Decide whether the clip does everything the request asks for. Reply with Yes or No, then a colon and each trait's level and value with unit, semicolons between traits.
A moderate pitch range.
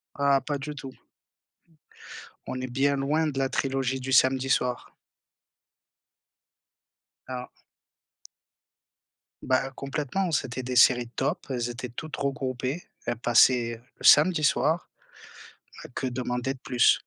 No: narrow, 1.9 semitones